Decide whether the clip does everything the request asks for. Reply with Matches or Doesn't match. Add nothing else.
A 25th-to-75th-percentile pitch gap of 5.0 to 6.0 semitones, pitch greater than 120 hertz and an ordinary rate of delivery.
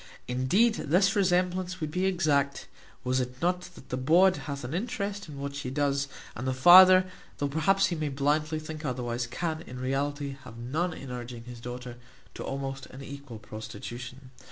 Matches